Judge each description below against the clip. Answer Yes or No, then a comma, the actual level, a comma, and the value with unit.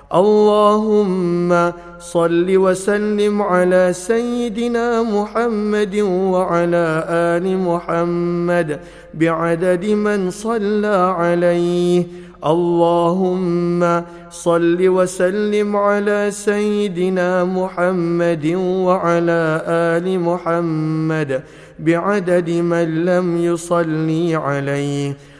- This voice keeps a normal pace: No, slow, 65 wpm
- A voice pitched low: No, medium, 175 Hz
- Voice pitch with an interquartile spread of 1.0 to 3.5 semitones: Yes, average, 2.8 semitones